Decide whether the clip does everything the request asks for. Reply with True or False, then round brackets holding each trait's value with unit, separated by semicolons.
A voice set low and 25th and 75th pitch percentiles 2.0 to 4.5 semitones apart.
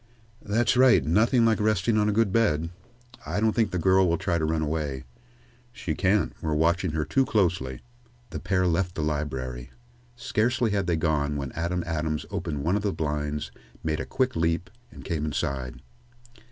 False (85 Hz; 5.2 semitones)